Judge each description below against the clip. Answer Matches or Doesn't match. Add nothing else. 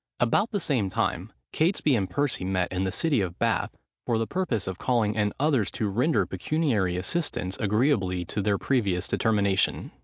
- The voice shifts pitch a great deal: Matches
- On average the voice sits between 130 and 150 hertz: Doesn't match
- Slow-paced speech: Doesn't match